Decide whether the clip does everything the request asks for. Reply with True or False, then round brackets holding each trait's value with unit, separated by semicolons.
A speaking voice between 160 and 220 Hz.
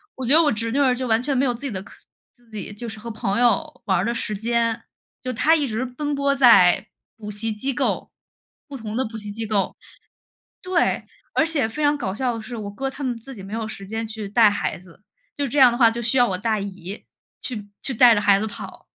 False (230 Hz)